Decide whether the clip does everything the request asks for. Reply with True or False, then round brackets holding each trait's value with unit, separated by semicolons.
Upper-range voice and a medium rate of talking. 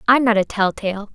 False (215 Hz; 265 wpm)